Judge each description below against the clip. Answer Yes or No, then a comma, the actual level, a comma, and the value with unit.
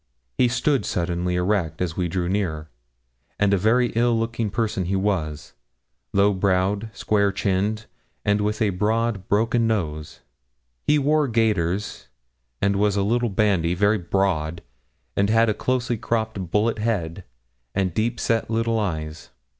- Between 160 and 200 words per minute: No, average, 145 wpm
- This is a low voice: Yes, low, 100 Hz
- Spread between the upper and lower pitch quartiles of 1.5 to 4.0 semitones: Yes, average, 3.7 semitones